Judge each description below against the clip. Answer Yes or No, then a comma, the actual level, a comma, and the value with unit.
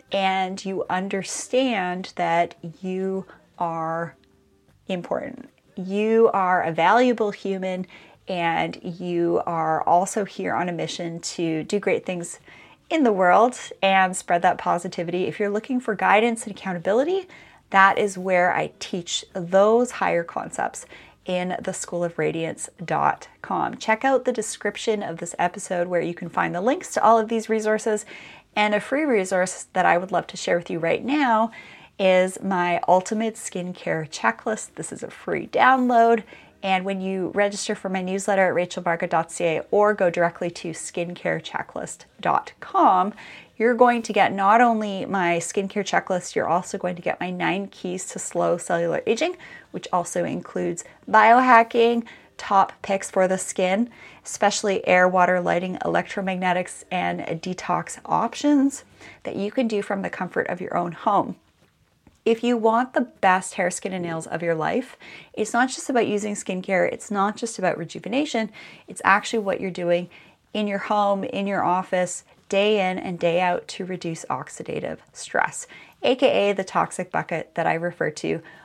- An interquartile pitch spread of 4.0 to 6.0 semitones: No, average, 3.5 semitones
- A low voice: No, high, 190 Hz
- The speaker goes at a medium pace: Yes, average, 155 wpm